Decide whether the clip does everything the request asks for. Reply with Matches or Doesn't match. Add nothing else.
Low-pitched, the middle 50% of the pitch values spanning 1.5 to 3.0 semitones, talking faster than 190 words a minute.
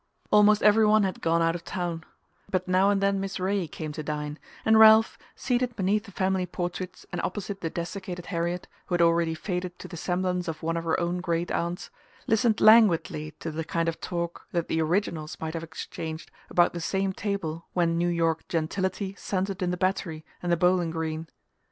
Doesn't match